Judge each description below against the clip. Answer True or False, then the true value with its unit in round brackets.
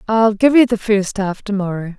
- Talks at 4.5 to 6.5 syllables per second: True (4.9 syllables/s)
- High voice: True (210 Hz)